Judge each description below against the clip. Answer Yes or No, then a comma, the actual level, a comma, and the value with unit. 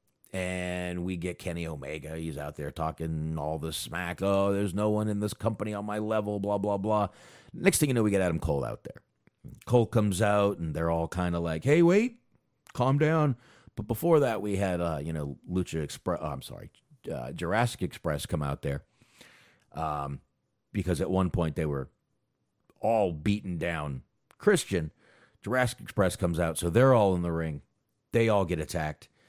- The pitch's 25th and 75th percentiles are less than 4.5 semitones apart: No, average, 5.2 semitones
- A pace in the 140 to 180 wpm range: No, average, 190 wpm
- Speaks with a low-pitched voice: Yes, very low, 95 Hz